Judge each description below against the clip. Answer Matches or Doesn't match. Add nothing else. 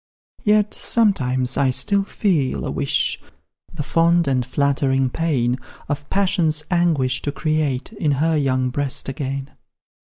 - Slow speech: Matches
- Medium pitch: Matches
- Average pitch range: Matches